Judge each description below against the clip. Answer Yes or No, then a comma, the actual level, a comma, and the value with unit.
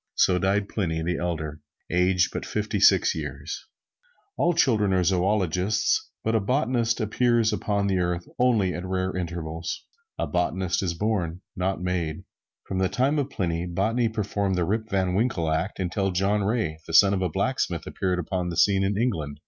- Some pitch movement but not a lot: Yes, average, 3.4 semitones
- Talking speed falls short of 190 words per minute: Yes, average, 175 wpm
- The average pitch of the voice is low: Yes, very low, 95 Hz